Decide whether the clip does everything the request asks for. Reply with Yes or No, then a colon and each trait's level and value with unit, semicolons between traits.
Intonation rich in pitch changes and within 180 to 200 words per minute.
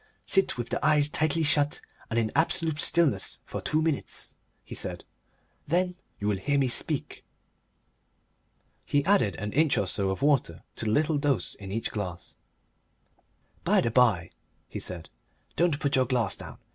No: wide, 6.5 semitones; average, 165 wpm